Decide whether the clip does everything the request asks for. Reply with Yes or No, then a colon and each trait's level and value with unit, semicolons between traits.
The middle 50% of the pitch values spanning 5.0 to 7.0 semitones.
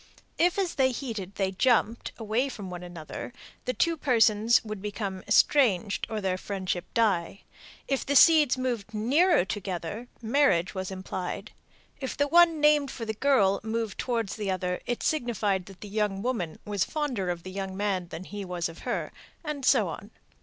Yes: average, 5.3 semitones